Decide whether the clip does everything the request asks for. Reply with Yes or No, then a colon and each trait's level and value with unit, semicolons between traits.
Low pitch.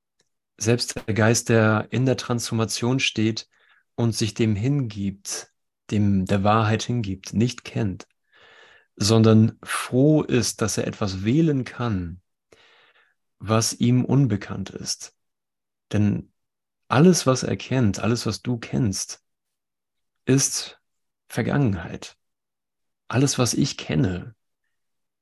Yes: low, 115 Hz